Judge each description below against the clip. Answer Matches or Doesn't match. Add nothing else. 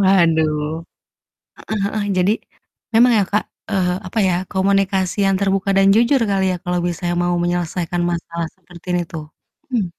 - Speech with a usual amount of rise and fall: Doesn't match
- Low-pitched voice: Doesn't match